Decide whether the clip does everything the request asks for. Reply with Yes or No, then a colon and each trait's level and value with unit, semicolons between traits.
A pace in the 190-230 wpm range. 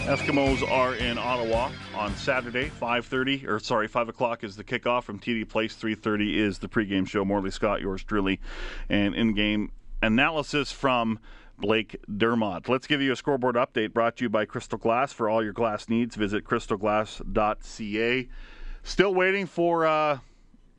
No: average, 160 wpm